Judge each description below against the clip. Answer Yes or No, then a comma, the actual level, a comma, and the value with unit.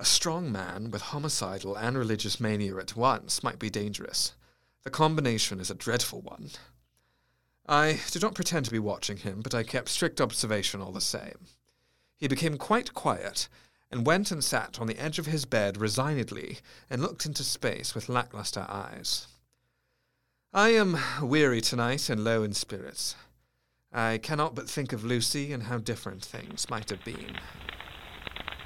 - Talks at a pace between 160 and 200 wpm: Yes, average, 165 wpm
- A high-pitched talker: No, low, 120 Hz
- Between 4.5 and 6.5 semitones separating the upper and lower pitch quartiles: Yes, average, 5.2 semitones